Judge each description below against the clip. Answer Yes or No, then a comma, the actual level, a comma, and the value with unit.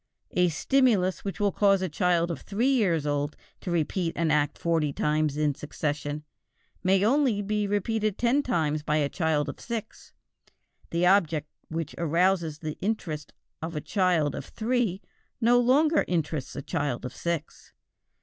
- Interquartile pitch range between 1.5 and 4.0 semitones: No, average, 5.3 semitones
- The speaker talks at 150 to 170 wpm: Yes, average, 160 wpm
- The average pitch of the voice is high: No, medium, 170 Hz